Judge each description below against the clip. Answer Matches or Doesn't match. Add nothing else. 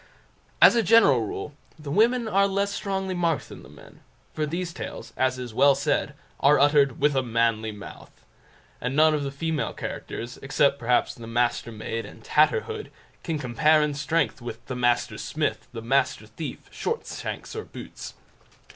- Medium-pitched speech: Matches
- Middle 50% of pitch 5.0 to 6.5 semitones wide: Matches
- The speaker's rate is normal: Matches